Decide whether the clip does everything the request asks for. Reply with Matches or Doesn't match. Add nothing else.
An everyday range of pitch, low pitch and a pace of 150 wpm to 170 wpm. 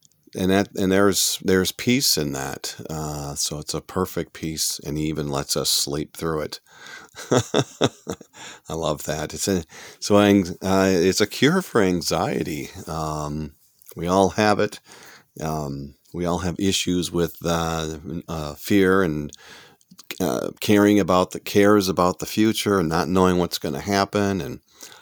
Matches